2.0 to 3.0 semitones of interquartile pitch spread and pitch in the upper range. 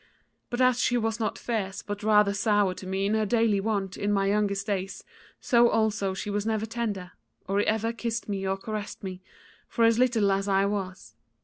Yes: narrow, 2.4 semitones; high, 205 Hz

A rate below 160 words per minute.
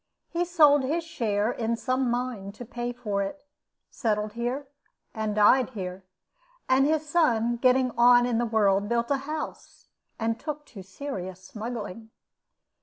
Yes: average, 150 wpm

